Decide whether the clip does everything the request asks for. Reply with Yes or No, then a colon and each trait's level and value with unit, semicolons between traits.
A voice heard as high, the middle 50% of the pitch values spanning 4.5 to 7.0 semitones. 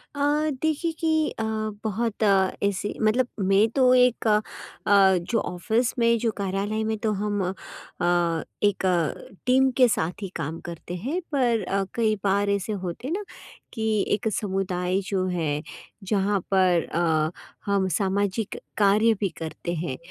No: high, 200 Hz; average, 3.8 semitones